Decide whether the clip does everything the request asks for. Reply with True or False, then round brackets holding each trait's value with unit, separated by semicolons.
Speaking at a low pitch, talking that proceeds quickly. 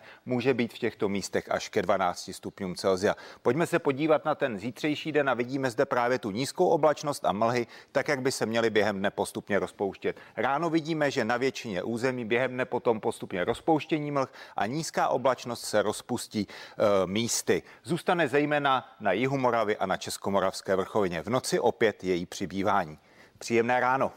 True (130 Hz; 175 wpm)